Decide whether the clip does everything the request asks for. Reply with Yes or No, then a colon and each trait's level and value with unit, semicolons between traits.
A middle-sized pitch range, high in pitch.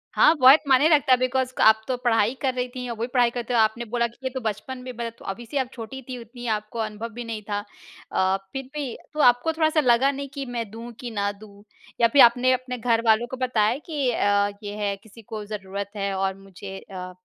Yes: average, 3.2 semitones; high, 235 Hz